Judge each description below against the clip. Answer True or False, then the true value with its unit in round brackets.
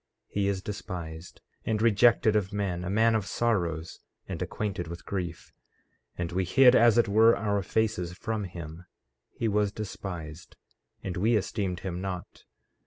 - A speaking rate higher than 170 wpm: False (160 wpm)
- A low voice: True (100 Hz)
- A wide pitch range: False (3.6 semitones)